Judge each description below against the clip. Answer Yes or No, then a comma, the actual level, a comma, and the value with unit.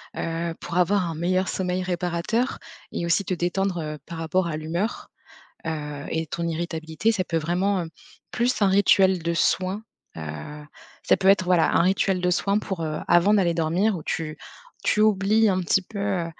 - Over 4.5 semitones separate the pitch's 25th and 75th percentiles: No, average, 2.8 semitones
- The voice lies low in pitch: No, medium, 180 Hz